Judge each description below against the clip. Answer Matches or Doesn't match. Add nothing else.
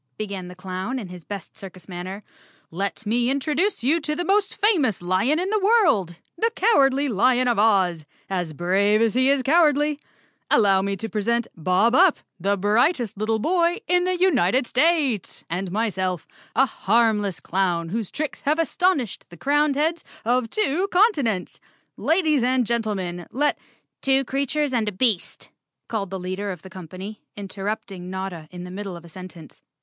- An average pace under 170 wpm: Doesn't match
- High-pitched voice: Matches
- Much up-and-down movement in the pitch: Matches